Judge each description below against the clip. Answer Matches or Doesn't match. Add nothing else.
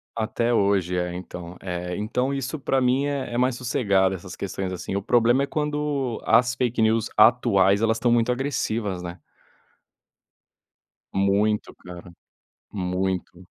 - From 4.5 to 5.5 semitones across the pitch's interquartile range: Matches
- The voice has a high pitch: Doesn't match